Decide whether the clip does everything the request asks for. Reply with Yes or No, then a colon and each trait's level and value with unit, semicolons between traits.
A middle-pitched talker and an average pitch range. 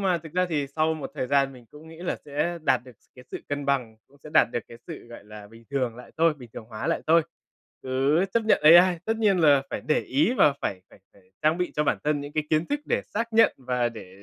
Yes: medium, 145 Hz; average, 4.9 semitones